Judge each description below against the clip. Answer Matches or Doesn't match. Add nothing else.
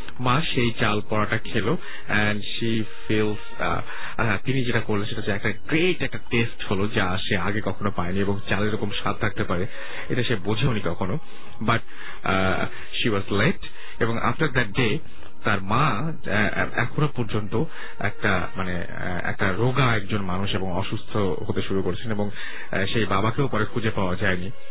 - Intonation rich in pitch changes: Doesn't match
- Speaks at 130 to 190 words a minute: Matches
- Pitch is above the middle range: Doesn't match